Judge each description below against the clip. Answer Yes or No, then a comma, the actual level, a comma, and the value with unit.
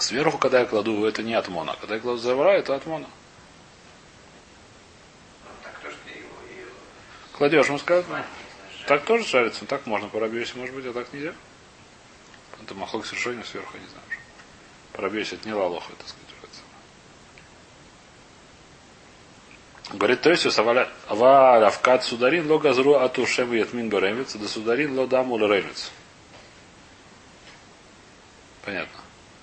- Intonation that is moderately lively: Yes, average, 3.1 semitones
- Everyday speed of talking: No, slow, 105 wpm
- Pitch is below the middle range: Yes, low, 125 Hz